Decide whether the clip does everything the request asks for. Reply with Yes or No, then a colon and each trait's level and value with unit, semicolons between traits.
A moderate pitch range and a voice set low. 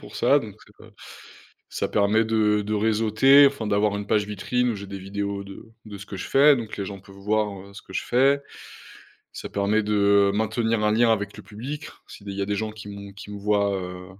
No: narrow, 1.7 semitones; low, 105 Hz